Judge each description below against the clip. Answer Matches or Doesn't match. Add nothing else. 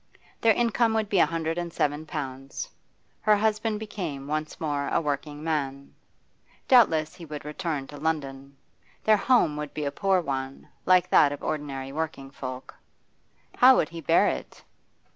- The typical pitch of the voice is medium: Matches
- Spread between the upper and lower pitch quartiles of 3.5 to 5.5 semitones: Matches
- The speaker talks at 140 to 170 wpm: Matches